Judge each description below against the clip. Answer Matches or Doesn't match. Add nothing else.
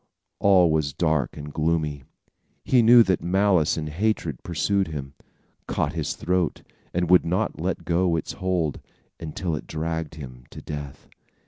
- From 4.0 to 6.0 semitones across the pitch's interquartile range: Doesn't match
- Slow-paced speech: Doesn't match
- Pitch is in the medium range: Doesn't match